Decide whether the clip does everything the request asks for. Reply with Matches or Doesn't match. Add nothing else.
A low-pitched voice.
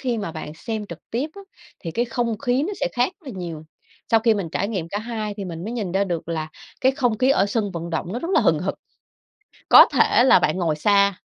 Doesn't match